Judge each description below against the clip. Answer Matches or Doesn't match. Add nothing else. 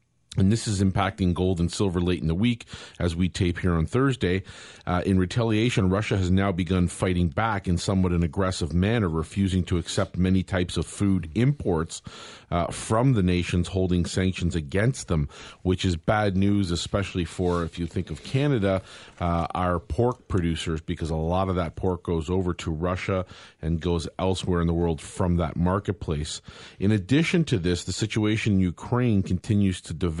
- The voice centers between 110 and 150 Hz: Doesn't match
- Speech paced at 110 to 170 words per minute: Doesn't match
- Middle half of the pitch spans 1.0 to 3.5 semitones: Matches